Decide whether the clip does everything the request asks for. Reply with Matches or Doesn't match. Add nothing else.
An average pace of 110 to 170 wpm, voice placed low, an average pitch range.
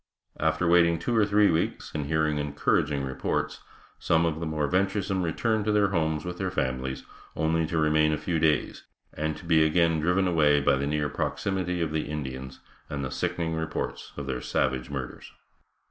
Doesn't match